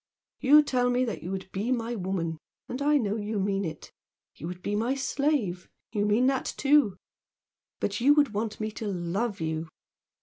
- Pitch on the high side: Yes, high, 215 Hz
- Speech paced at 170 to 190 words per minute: Yes, average, 180 wpm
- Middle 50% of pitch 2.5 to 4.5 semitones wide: No, average, 5.2 semitones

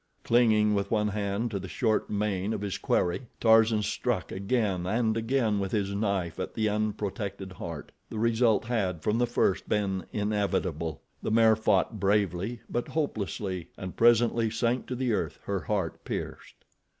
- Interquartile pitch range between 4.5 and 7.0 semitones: No, narrow, 2.6 semitones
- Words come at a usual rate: Yes, average, 160 wpm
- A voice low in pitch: Yes, low, 105 Hz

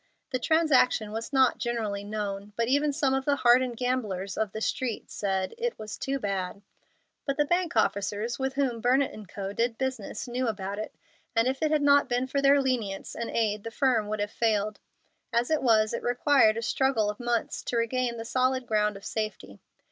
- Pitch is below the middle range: No, high, 235 Hz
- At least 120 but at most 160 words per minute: No, average, 200 wpm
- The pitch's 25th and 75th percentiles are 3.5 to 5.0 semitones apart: Yes, average, 3.8 semitones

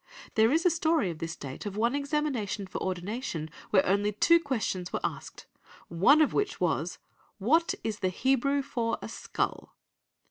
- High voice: Yes, high, 225 Hz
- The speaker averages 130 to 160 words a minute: No, average, 170 wpm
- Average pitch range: No, wide, 7.1 semitones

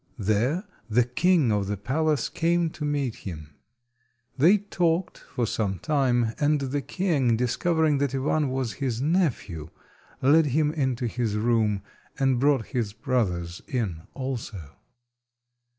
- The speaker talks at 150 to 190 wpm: No, slow, 135 wpm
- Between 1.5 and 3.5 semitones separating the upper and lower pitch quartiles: No, average, 5.2 semitones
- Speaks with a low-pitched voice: Yes, low, 130 Hz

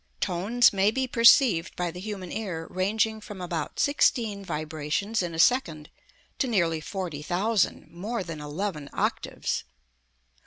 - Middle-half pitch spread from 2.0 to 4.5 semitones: No, average, 4.9 semitones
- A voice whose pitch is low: No, high, 190 Hz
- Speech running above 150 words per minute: No, average, 140 wpm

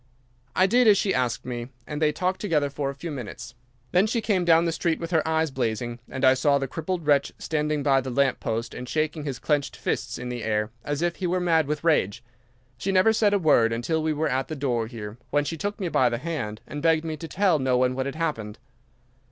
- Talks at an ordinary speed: No, fast, 245 wpm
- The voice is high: No, medium, 150 Hz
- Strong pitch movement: No, average, 4.7 semitones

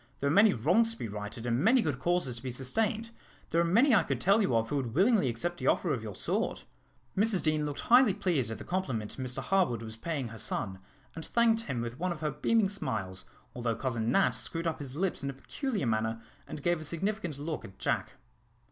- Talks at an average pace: No, fast, 230 wpm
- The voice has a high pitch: No, medium, 150 Hz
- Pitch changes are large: Yes, wide, 8.4 semitones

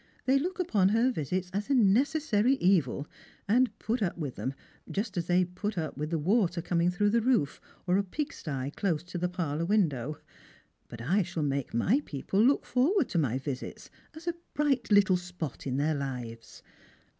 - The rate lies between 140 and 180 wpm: No, average, 190 wpm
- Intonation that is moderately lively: No, wide, 6.9 semitones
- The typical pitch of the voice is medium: Yes, medium, 180 Hz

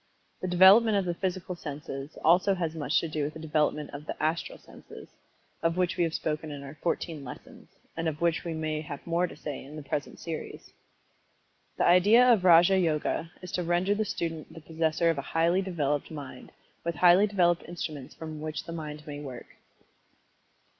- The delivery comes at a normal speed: Yes, average, 195 wpm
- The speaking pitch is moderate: Yes, medium, 165 Hz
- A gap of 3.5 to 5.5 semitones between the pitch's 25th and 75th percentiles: No, average, 2.8 semitones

